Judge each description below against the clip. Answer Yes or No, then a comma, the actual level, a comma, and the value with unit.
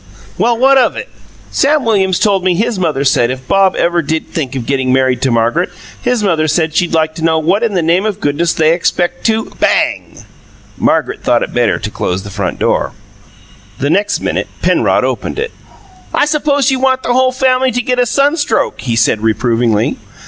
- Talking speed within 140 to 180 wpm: No, average, 200 wpm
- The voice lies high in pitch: No, medium, 175 Hz